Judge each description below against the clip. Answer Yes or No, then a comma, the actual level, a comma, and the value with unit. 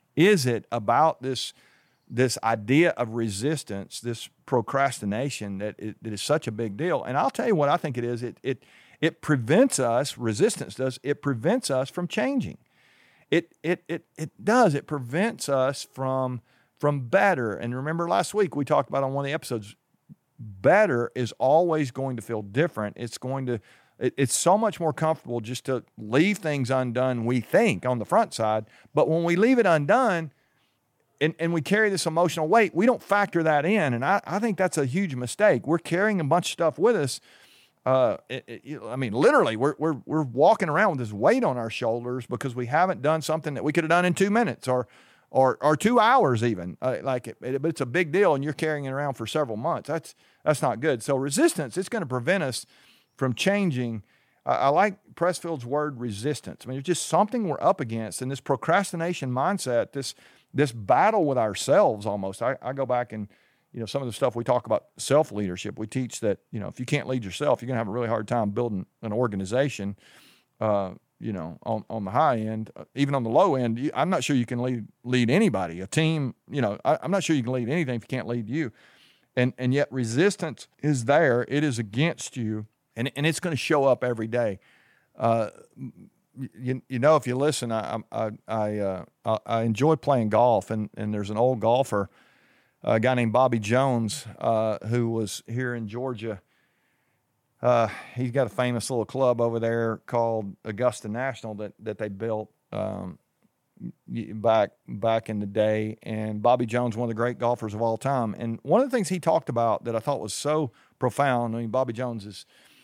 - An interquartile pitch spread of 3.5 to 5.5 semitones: Yes, average, 5.2 semitones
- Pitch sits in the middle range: No, low, 130 Hz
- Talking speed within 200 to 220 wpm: Yes, fast, 205 wpm